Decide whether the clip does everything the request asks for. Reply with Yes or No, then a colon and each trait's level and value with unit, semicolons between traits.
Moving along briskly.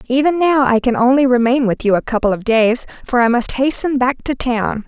Yes: fast, 235 wpm